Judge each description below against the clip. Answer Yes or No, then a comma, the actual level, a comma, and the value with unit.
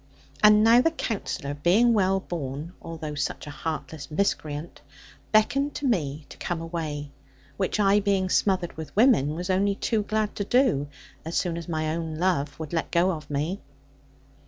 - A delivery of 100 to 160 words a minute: No, average, 170 wpm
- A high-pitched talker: No, medium, 175 Hz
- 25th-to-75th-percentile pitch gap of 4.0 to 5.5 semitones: Yes, average, 4.7 semitones